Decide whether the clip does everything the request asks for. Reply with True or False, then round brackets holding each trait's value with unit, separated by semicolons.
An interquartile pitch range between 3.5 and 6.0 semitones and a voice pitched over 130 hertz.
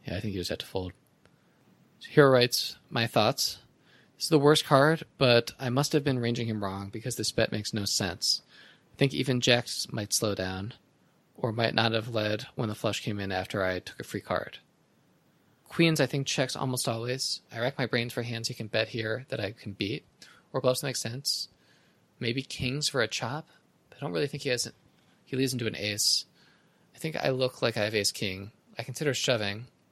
False (3.9 semitones; 120 Hz)